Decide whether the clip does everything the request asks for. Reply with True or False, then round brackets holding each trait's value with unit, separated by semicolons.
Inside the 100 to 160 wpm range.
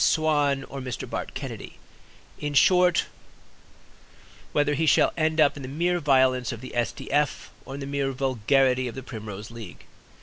False (175 wpm)